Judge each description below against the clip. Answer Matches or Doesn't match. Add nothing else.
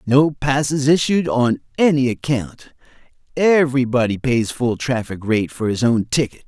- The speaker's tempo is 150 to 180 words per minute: Doesn't match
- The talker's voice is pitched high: Doesn't match